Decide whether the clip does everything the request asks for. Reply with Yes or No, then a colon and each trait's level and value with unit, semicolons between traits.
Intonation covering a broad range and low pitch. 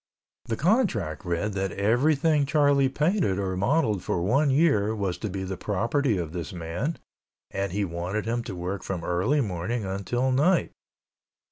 Yes: wide, 6.9 semitones; low, 105 Hz